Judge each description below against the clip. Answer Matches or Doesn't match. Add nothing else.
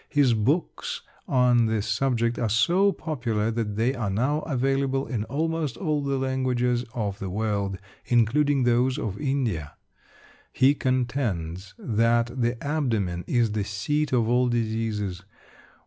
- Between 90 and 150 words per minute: Matches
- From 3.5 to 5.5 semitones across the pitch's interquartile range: Matches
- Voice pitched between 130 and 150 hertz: Doesn't match